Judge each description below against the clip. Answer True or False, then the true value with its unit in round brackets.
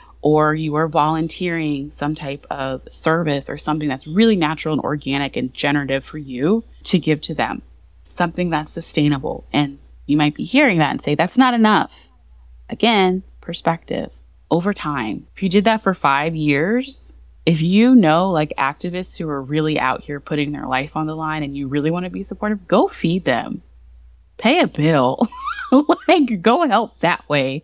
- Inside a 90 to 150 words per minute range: False (180 wpm)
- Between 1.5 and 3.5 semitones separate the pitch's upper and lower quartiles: False (4.7 semitones)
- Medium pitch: True (155 Hz)